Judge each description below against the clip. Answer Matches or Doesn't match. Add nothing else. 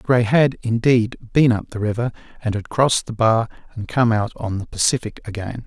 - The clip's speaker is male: Matches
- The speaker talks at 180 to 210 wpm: Matches